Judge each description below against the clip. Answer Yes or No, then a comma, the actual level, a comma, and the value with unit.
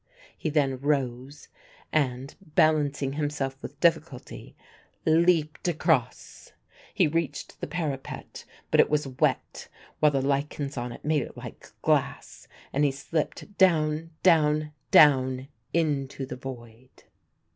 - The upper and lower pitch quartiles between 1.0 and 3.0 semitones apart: Yes, narrow, 2.6 semitones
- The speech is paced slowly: Yes, slow, 125 wpm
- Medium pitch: Yes, medium, 145 Hz